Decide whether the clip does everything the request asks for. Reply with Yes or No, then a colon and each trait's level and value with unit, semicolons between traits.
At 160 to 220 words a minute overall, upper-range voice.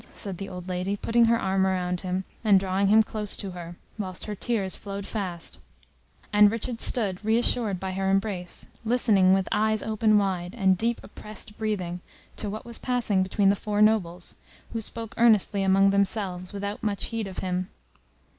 Yes: average, 175 wpm; high, 200 Hz